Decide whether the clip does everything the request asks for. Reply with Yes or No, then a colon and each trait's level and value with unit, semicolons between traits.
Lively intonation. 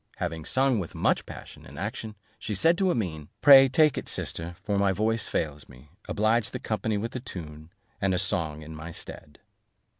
Yes: wide, 6.4 semitones